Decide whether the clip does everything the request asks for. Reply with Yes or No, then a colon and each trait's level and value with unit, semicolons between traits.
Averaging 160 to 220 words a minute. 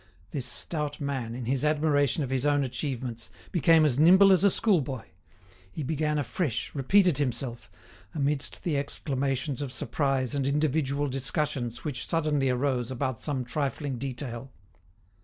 No: average, 140 wpm